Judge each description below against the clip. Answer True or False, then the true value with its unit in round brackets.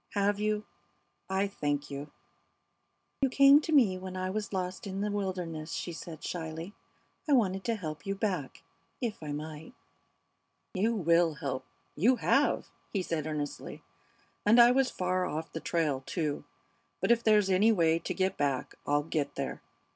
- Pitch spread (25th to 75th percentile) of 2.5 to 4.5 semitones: False (4.9 semitones)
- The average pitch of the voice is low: False (185 Hz)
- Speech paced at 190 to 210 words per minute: False (170 wpm)